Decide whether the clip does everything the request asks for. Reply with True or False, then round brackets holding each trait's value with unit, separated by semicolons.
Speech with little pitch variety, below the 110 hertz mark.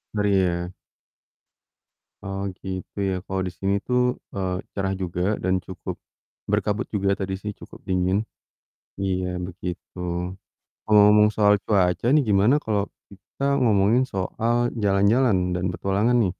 True (2.1 semitones; 95 Hz)